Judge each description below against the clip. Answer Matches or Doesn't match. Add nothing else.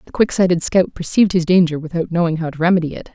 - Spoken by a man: Doesn't match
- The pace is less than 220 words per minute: Doesn't match